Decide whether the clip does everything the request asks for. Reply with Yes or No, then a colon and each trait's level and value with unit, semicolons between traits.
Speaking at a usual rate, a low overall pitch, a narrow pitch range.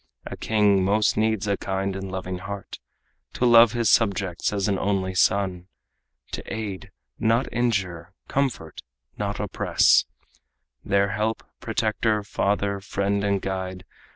No: slow, 130 wpm; low, 100 Hz; narrow, 2.3 semitones